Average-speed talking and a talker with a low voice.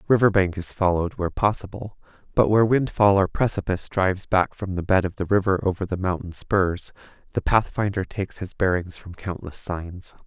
Yes: average, 180 wpm; very low, 95 Hz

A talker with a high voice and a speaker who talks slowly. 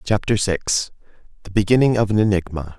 No: low, 100 Hz; slow, 130 wpm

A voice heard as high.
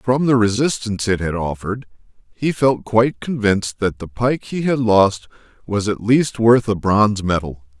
No: low, 110 Hz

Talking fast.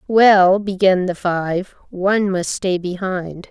No: slow, 135 wpm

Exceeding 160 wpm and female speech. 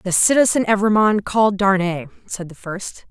No: average, 155 wpm; female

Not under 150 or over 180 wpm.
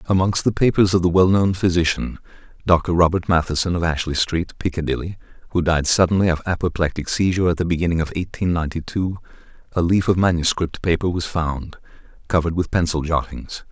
Yes: average, 165 wpm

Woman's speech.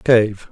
No: male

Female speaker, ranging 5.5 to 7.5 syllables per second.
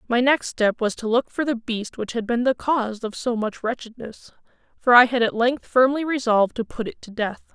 No: female; 5.3 syllables/s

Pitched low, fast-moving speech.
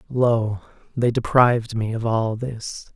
No: low, 115 Hz; average, 140 wpm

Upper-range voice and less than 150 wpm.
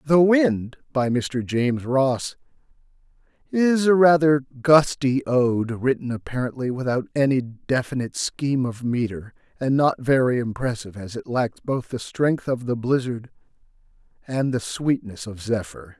No: low, 130 Hz; average, 140 wpm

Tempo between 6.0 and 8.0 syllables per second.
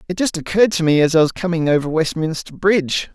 Yes: 6.5 syllables/s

